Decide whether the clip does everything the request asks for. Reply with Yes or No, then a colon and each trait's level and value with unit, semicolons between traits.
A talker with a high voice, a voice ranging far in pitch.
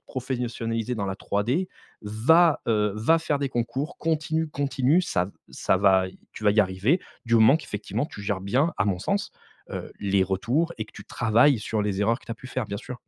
No: low, 115 Hz; wide, 5.7 semitones